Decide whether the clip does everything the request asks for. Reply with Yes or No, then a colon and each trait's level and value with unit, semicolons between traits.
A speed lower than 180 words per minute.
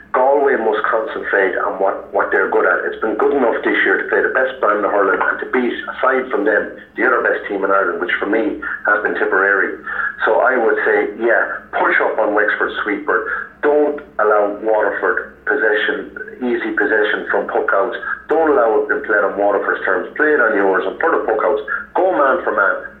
No: average, 200 wpm